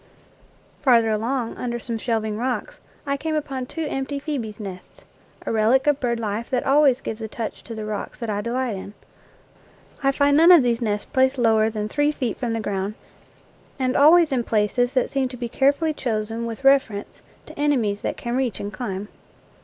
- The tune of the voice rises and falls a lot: No, average, 3.9 semitones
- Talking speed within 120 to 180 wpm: No, average, 195 wpm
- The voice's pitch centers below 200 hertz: No, high, 240 Hz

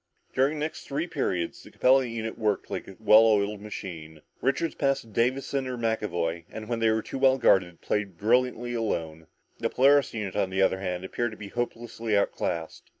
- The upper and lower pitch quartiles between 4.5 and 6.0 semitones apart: Yes, average, 4.8 semitones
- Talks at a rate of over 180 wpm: Yes, average, 195 wpm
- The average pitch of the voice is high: No, low, 110 Hz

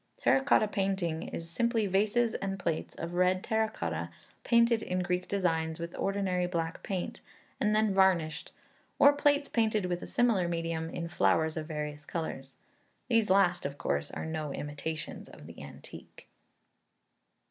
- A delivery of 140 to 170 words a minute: Yes, average, 155 wpm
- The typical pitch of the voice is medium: Yes, medium, 180 Hz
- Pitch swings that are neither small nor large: Yes, average, 4.6 semitones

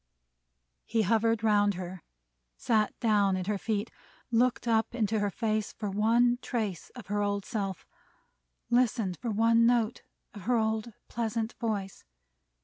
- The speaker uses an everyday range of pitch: No, narrow, 2.1 semitones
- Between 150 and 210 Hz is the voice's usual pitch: No, high, 220 Hz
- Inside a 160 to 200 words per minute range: No, average, 140 wpm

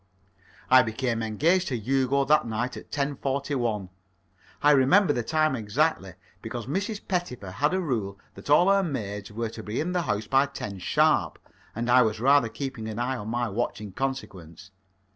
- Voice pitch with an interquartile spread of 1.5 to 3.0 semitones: No, average, 4.9 semitones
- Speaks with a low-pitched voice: Yes, low, 125 Hz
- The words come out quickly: No, average, 180 wpm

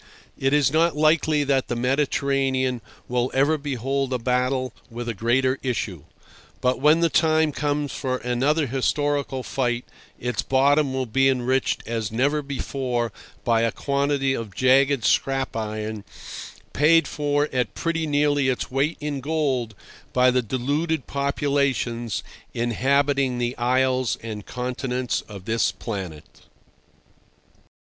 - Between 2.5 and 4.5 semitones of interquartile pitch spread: Yes, average, 2.8 semitones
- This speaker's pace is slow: Yes, slow, 130 wpm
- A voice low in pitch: Yes, low, 130 Hz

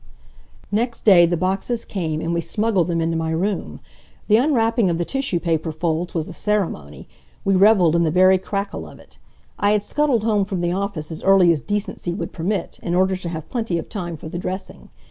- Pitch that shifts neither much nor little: Yes, average, 3.7 semitones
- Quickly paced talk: Yes, fast, 210 wpm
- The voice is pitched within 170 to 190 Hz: Yes, medium, 185 Hz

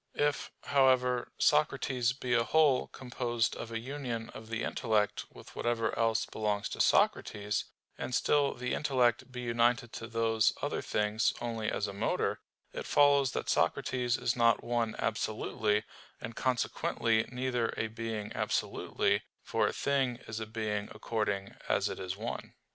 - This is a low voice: Yes, low, 115 Hz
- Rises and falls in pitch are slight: Yes, narrow, 2.3 semitones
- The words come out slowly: No, average, 155 wpm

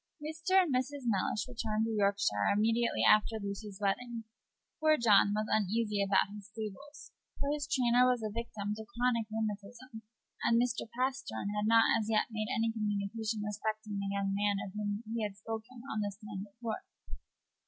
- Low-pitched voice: No, high, 220 Hz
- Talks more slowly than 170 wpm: No, average, 175 wpm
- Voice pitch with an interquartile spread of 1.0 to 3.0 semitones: Yes, narrow, 2.6 semitones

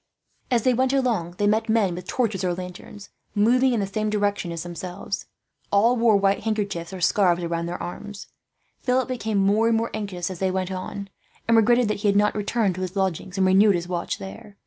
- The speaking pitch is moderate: No, high, 200 Hz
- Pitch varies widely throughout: No, average, 3.2 semitones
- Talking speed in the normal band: No, fast, 215 wpm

